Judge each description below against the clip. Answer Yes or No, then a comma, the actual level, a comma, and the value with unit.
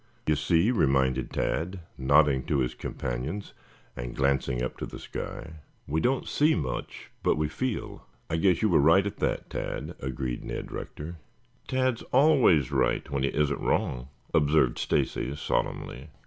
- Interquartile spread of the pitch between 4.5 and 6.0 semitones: Yes, wide, 5.5 semitones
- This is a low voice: Yes, very low, 75 Hz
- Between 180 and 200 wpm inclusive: No, average, 155 wpm